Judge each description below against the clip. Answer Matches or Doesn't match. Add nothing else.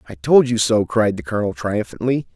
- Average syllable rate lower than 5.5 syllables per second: Doesn't match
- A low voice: Matches